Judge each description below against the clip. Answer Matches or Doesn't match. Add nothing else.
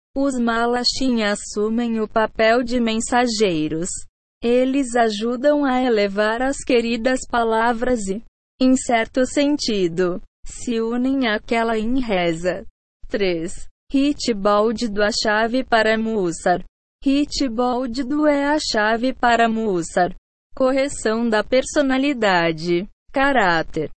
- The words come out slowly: Matches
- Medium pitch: Doesn't match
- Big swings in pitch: Doesn't match